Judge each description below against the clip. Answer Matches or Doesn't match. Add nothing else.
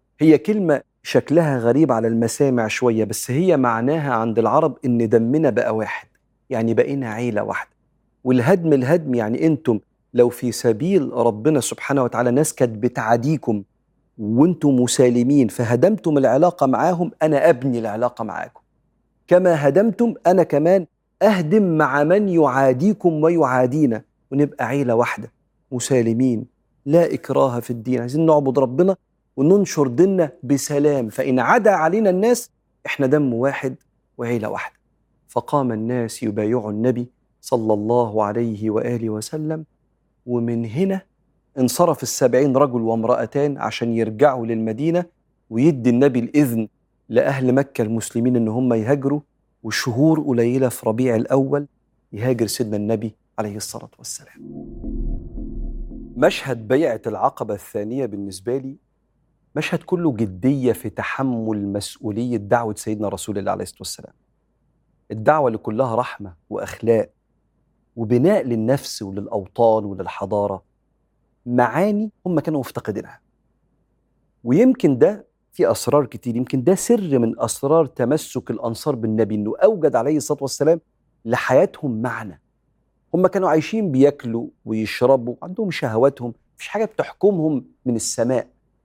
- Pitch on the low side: Matches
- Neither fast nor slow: Matches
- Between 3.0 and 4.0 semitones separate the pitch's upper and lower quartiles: Doesn't match